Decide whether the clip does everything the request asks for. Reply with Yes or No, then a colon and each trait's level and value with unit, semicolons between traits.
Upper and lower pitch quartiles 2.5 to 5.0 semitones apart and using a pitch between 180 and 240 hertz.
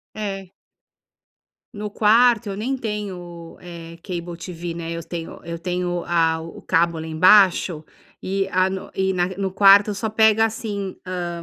Yes: average, 3.4 semitones; medium, 185 Hz